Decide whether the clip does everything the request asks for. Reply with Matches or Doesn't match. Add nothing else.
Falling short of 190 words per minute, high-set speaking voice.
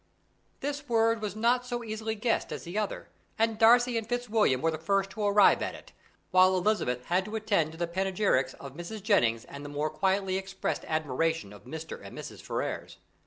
Doesn't match